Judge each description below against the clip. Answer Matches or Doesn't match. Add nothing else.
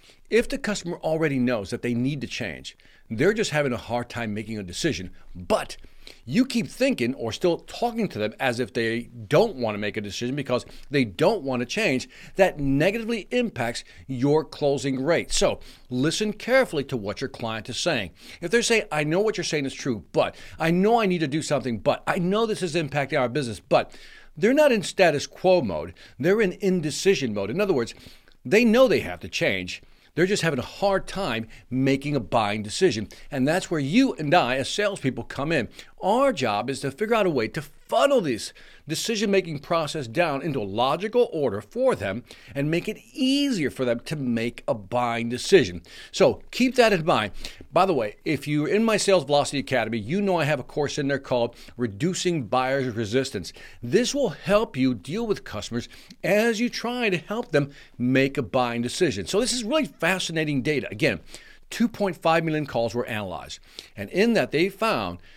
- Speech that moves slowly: Doesn't match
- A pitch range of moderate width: Doesn't match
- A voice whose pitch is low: Doesn't match